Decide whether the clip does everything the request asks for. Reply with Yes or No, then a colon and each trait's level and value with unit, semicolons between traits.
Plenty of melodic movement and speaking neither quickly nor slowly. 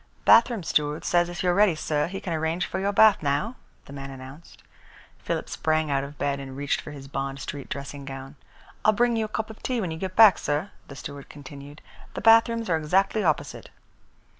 No: wide, 6.1 semitones; fast, 215 wpm